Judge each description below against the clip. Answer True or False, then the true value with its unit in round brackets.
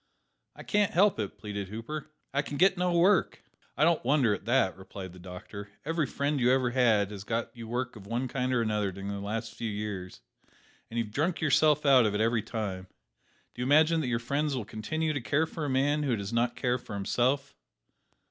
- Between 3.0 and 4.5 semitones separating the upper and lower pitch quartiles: False (5.6 semitones)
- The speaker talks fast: True (215 wpm)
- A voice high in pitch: False (120 Hz)